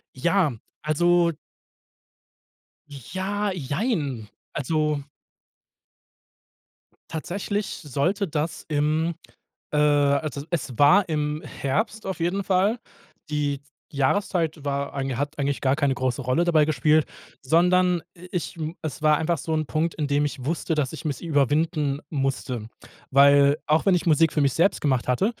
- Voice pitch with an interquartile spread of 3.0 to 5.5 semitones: Yes, average, 3.4 semitones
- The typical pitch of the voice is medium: Yes, medium, 155 Hz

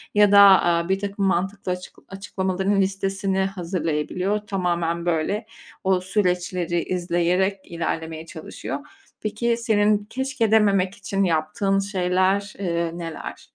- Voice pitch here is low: No, high, 190 Hz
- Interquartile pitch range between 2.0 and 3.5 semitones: Yes, narrow, 2.6 semitones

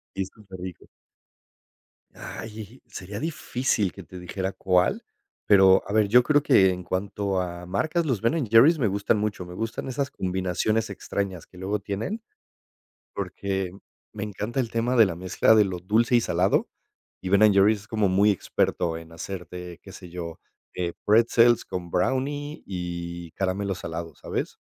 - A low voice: Yes, low, 100 Hz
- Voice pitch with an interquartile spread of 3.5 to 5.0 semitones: Yes, average, 3.8 semitones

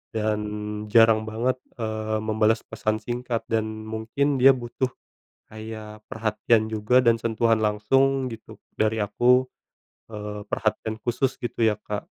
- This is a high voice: No, low, 110 Hz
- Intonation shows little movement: Yes, narrow, 1.8 semitones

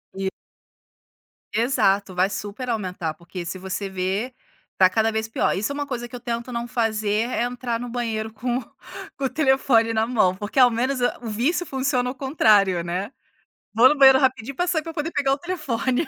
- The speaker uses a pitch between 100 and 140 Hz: No, high, 235 Hz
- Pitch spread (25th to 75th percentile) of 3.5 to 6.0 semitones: Yes, average, 4.3 semitones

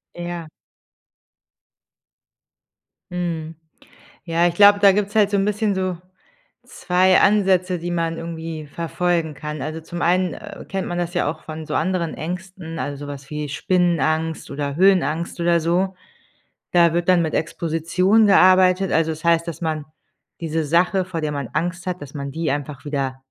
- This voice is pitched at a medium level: Yes, medium, 170 Hz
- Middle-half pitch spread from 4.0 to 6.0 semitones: No, average, 2.7 semitones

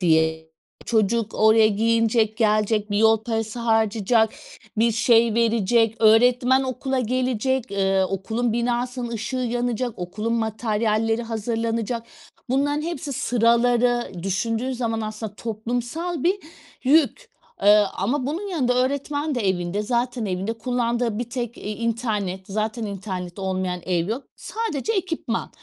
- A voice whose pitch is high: Yes, high, 230 Hz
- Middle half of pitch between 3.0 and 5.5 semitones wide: No, narrow, 2.6 semitones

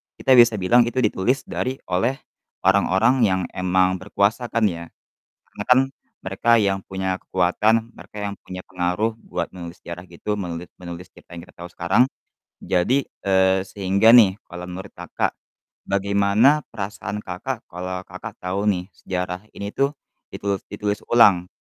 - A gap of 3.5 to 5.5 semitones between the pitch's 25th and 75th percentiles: No, average, 3.1 semitones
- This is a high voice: No, very low, 95 Hz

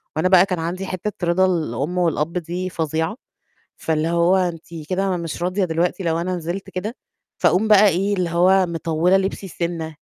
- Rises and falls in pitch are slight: Yes, narrow, 2.2 semitones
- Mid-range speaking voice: Yes, medium, 175 Hz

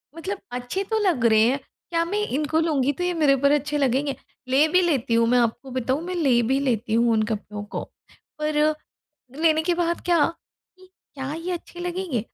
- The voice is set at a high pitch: Yes, very high, 285 Hz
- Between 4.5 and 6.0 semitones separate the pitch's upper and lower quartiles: Yes, wide, 5.6 semitones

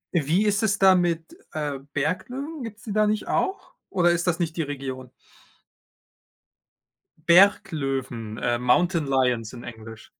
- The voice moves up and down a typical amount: No, wide, 7.1 semitones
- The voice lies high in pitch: No, medium, 165 Hz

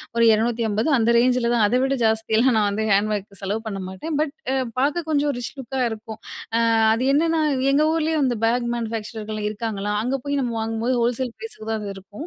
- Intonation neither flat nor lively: Yes, average, 4.0 semitones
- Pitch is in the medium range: No, high, 235 Hz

